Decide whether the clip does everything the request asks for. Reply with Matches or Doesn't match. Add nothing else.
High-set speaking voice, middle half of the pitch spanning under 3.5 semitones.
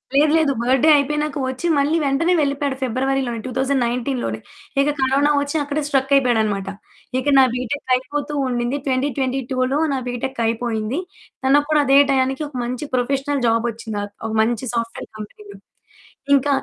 Matches